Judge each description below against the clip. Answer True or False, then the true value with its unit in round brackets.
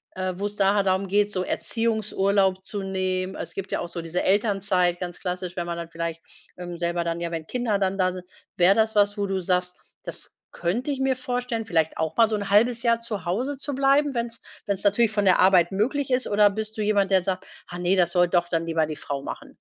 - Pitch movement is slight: False (3.5 semitones)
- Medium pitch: False (195 Hz)